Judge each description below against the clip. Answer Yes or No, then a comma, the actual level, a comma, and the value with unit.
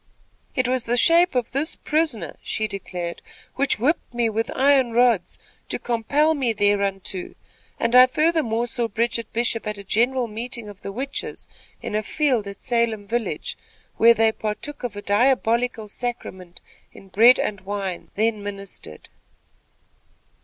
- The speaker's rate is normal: Yes, average, 150 wpm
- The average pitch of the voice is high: Yes, high, 230 Hz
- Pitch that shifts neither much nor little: Yes, average, 3.6 semitones